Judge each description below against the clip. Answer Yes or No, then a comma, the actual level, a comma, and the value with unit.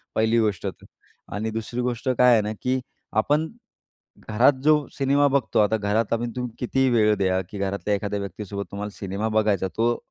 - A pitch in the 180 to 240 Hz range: No, low, 110 Hz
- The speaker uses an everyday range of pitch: Yes, average, 3.3 semitones